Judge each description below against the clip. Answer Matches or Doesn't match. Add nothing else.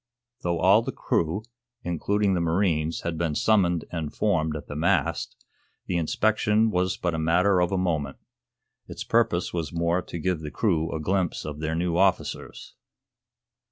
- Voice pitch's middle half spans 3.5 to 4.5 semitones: Doesn't match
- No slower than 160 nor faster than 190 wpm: Matches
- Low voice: Matches